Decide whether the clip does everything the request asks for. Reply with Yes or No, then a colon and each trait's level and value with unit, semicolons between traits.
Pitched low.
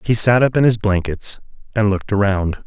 Yes: low, 105 Hz